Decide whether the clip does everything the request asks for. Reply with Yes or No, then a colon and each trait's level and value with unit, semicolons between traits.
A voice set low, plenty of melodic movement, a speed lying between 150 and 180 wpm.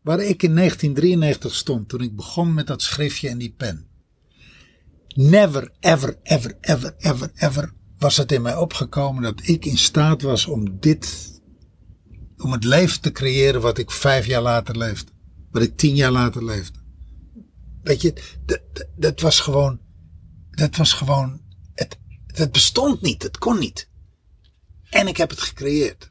Yes: low, 130 Hz; wide, 7.6 semitones; average, 165 wpm